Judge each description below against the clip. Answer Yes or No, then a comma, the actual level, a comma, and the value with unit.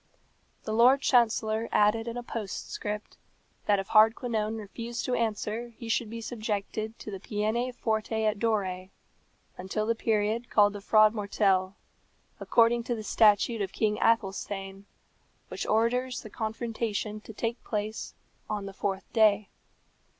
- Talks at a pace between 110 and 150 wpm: Yes, average, 140 wpm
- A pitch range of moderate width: No, narrow, 1.9 semitones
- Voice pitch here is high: Yes, high, 215 Hz